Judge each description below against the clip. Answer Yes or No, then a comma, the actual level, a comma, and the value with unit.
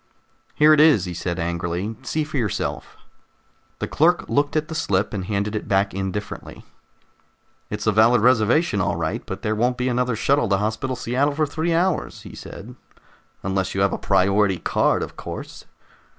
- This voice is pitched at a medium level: No, low, 110 Hz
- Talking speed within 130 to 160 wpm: No, average, 180 wpm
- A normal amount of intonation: No, wide, 6.6 semitones